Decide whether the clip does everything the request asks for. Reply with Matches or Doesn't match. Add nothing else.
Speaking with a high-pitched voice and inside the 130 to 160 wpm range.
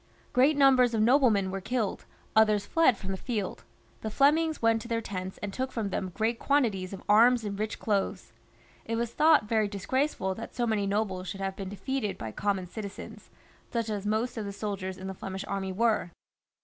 Doesn't match